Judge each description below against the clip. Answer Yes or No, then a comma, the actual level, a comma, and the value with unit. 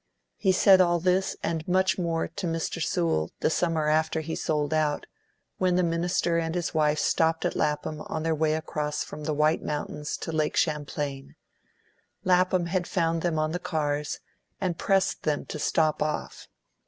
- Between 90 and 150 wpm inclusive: No, average, 175 wpm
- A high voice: No, medium, 160 Hz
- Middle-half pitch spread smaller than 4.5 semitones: Yes, narrow, 2.4 semitones